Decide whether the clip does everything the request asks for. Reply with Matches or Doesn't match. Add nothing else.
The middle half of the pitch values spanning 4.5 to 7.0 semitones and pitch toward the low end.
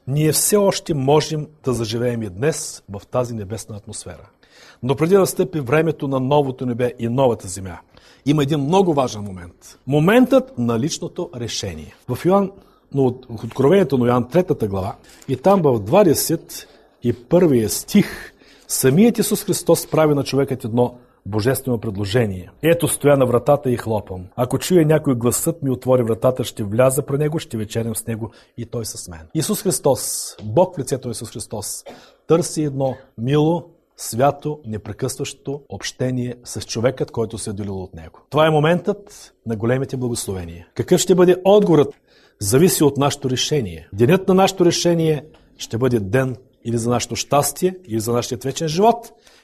Matches